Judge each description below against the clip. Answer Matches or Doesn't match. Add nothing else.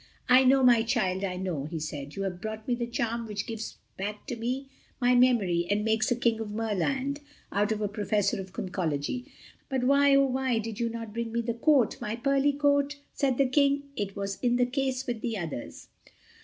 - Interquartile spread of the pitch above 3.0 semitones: Matches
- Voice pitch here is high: Matches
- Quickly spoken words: Matches